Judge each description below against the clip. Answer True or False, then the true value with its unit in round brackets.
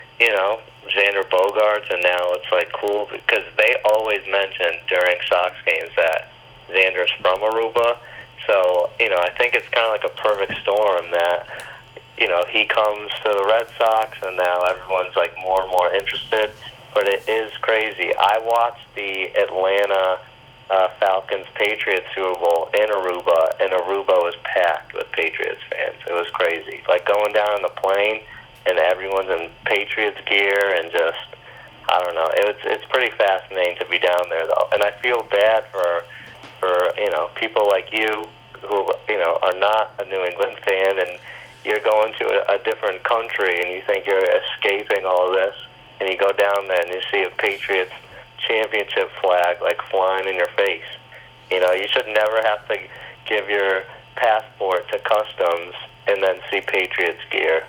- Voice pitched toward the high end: False (110 Hz)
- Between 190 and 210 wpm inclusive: False (175 wpm)